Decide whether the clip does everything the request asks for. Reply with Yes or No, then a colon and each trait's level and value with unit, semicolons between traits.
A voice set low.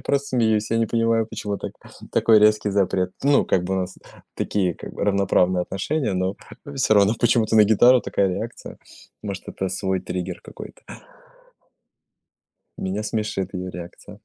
Yes: low, 105 Hz